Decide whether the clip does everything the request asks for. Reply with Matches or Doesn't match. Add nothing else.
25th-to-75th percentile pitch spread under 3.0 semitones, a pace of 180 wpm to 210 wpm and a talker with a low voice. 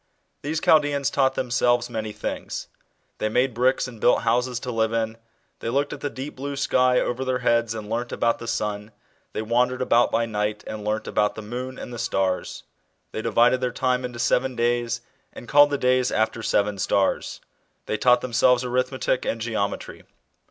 Matches